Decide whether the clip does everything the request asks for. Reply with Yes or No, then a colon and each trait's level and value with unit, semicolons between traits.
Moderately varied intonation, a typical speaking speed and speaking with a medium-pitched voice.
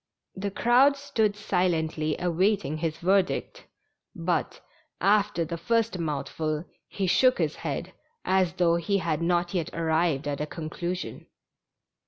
No: average, 3.8 semitones; slow, 130 wpm; medium, 175 Hz